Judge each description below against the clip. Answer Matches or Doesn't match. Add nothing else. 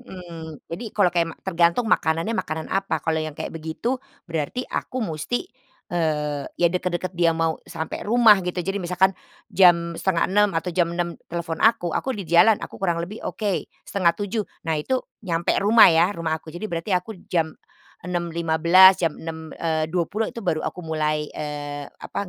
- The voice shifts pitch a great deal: Doesn't match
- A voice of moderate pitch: Matches